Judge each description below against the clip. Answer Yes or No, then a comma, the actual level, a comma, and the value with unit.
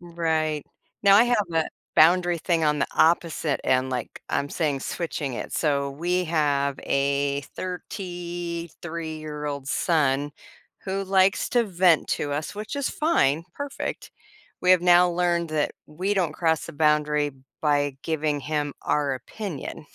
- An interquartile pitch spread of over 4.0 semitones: No, average, 3.4 semitones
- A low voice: No, medium, 160 Hz